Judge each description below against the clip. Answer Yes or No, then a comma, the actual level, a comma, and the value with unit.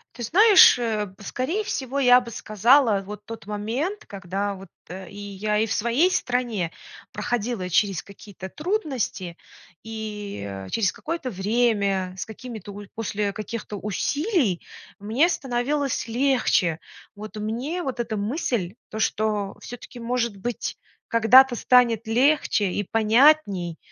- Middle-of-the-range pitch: No, high, 225 Hz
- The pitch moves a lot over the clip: No, average, 3.8 semitones